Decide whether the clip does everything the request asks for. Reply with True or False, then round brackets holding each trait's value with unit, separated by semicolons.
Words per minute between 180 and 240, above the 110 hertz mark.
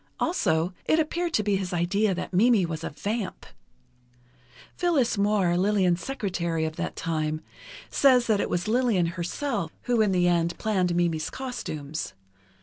False (150 wpm; 190 Hz)